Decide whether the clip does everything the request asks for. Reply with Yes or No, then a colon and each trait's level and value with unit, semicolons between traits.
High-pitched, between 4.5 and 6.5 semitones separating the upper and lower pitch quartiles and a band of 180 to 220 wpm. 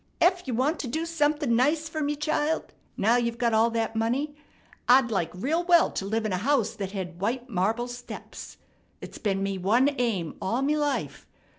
Yes: high, 245 Hz; average, 5.2 semitones; average, 195 wpm